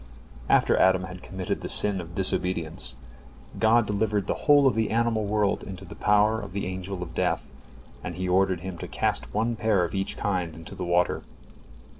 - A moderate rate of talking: Yes, average, 190 wpm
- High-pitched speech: No, very low, 95 Hz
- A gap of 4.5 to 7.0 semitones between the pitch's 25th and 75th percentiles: No, average, 3.0 semitones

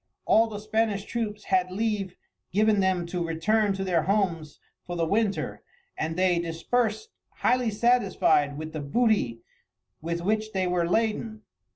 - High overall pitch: Yes, high, 195 Hz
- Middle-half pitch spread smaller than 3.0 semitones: No, average, 4.2 semitones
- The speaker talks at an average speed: Yes, average, 150 wpm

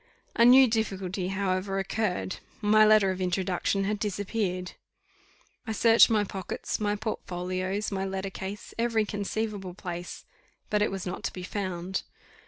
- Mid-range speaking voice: No, high, 195 Hz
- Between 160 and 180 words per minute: No, average, 145 wpm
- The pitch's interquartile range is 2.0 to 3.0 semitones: Yes, narrow, 2.4 semitones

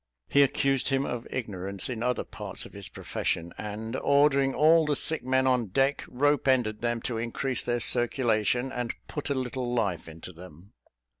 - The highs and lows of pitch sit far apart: No, average, 3.7 semitones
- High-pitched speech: No, low, 125 Hz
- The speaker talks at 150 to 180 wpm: Yes, average, 175 wpm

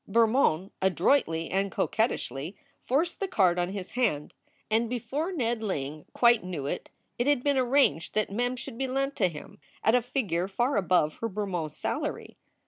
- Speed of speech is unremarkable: Yes, average, 170 wpm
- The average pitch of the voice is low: No, high, 215 Hz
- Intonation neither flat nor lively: No, wide, 6.0 semitones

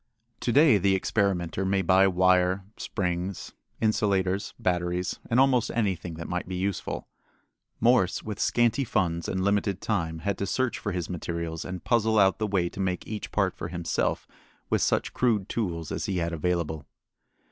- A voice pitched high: No, very low, 95 Hz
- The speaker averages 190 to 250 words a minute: No, average, 170 wpm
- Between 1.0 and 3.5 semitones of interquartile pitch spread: Yes, average, 3.1 semitones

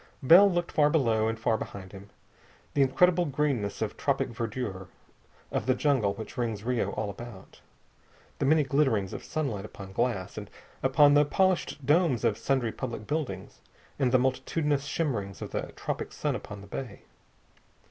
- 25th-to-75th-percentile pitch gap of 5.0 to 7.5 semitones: Yes, wide, 5.6 semitones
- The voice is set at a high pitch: No, low, 125 Hz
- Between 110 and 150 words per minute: No, average, 165 wpm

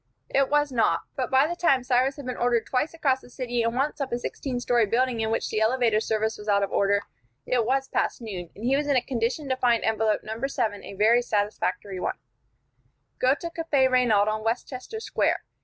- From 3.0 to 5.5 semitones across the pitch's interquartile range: Yes, average, 3.4 semitones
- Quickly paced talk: Yes, fast, 220 wpm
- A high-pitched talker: Yes, high, 245 Hz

